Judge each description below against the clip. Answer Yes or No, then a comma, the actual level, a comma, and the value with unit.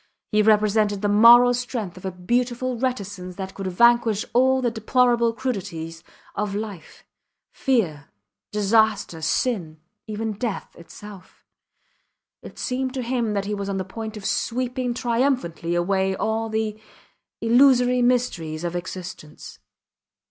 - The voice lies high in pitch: Yes, high, 215 Hz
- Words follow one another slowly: Yes, slow, 125 wpm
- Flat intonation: No, average, 4.2 semitones